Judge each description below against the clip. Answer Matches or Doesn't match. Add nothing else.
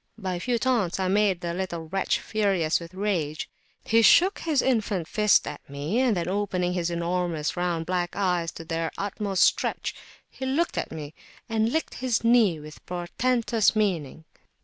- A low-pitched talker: Doesn't match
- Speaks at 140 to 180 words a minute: Matches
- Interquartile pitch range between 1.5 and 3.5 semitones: Doesn't match